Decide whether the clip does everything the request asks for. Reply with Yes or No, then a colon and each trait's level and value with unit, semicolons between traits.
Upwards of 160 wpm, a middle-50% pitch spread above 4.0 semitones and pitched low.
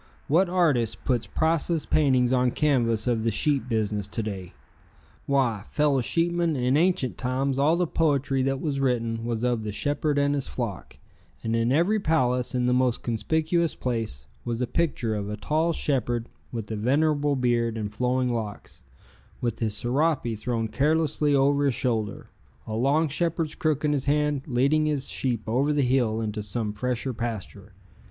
Yes: average, 170 wpm; average, 4.4 semitones; low, 130 Hz